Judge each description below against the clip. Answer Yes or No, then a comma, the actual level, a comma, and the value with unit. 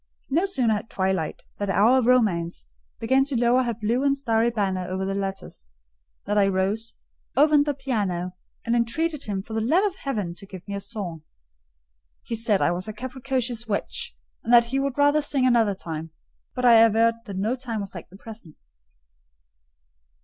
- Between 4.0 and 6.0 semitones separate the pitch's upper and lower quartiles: Yes, average, 4.7 semitones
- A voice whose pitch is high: Yes, high, 225 Hz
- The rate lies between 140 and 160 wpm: No, average, 185 wpm